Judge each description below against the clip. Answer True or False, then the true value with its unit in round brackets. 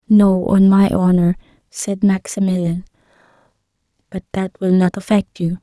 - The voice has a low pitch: False (190 Hz)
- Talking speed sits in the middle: False (130 wpm)